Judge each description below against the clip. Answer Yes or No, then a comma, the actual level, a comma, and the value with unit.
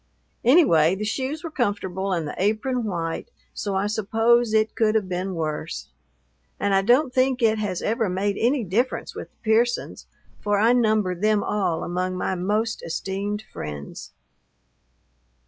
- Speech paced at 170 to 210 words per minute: No, average, 155 wpm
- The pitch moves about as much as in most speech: Yes, average, 3.6 semitones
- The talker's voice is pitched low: No, high, 210 Hz